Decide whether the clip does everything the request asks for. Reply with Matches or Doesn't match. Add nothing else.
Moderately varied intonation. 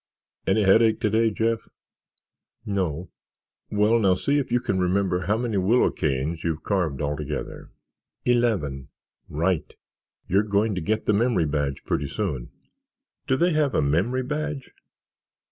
Doesn't match